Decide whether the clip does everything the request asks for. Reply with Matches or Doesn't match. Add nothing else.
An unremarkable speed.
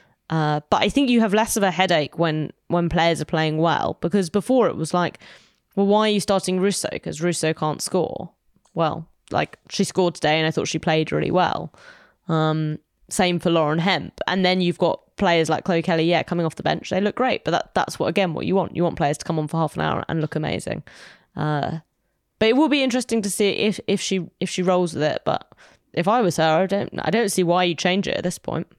Doesn't match